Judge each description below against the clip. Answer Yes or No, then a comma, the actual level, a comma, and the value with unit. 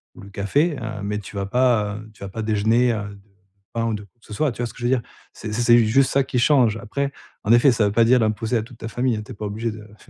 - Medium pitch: No, low, 115 Hz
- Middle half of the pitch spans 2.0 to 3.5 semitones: Yes, narrow, 2.6 semitones